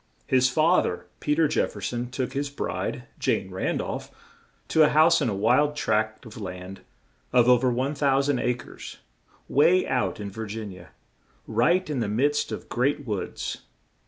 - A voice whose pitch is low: Yes, low, 125 Hz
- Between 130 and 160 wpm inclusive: No, average, 180 wpm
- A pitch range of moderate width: Yes, average, 5.0 semitones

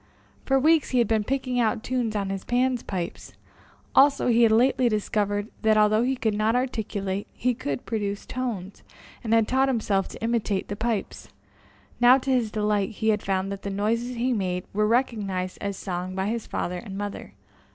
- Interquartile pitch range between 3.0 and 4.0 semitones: Yes, average, 3.5 semitones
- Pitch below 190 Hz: No, high, 220 Hz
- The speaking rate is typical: Yes, average, 190 wpm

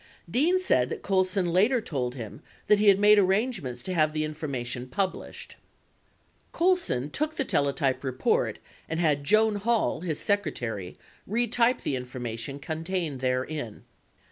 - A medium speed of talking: Yes, average, 145 wpm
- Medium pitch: Yes, medium, 160 Hz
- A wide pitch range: Yes, wide, 8.3 semitones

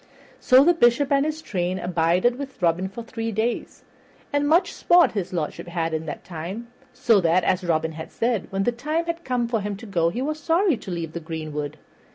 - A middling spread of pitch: No, wide, 7.5 semitones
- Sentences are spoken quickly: Yes, fast, 210 wpm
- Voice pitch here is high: Yes, high, 205 Hz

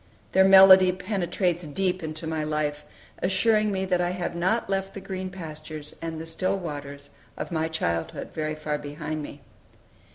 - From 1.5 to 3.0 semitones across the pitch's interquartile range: No, average, 3.6 semitones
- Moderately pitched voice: Yes, medium, 170 Hz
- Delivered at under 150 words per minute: No, average, 165 wpm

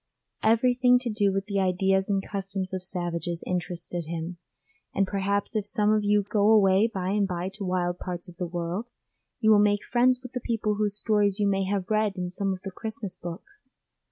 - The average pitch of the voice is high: Yes, high, 195 Hz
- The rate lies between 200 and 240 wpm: Yes, fast, 205 wpm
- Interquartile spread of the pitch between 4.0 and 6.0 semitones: No, average, 2.7 semitones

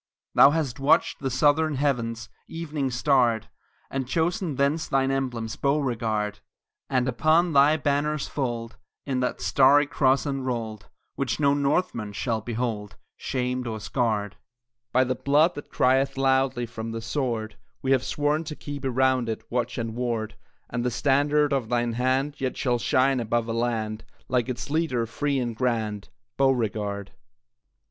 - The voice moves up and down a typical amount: Yes, average, 3.3 semitones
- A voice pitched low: Yes, low, 130 Hz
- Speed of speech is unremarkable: Yes, average, 155 wpm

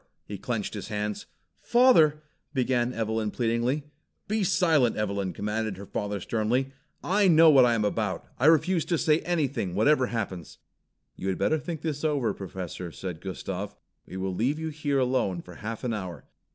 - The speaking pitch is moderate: No, low, 120 Hz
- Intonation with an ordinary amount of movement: No, wide, 6.9 semitones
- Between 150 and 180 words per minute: Yes, average, 175 wpm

